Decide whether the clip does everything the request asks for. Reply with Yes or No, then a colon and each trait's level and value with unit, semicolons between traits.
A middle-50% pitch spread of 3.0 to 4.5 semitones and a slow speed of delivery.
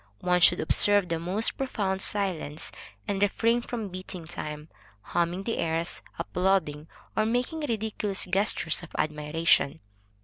Yes: average, 4.1 semitones; slow, 130 wpm